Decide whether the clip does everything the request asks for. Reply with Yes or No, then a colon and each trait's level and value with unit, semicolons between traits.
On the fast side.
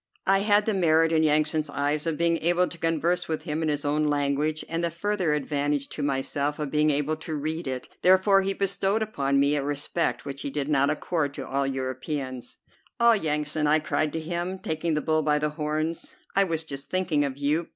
Yes: fast, 215 wpm